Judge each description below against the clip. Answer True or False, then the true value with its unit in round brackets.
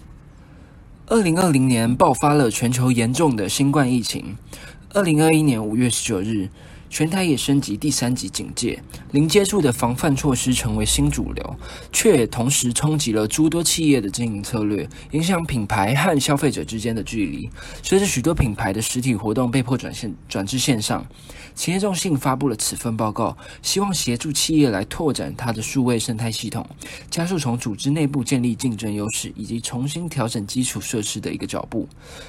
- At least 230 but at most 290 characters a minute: True (285 characters per minute)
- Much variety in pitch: False (4.5 semitones)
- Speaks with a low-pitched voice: True (125 Hz)